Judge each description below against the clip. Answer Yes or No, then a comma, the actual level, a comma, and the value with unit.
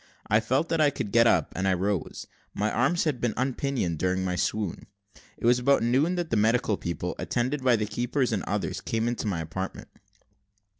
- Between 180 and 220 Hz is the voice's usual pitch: No, low, 115 Hz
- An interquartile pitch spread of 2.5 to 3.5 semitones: No, average, 4.7 semitones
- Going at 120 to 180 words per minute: No, average, 200 wpm